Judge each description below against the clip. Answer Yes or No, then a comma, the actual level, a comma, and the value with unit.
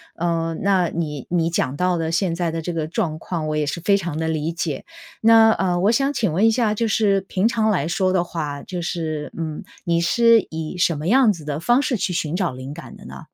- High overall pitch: No, medium, 170 Hz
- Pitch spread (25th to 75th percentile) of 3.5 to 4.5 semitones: Yes, average, 3.9 semitones